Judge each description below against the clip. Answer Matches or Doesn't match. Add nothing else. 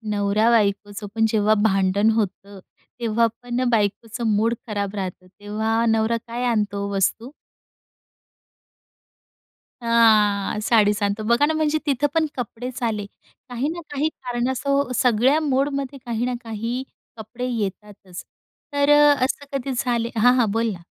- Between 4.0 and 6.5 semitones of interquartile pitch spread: Doesn't match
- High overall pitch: Matches